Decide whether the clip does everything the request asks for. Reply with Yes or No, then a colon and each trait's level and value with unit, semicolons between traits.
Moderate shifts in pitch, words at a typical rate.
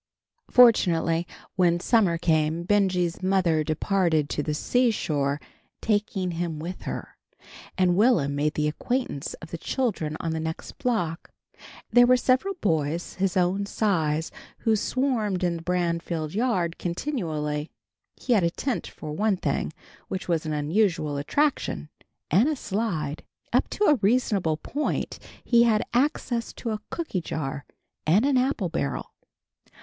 No: wide, 6.0 semitones; average, 145 wpm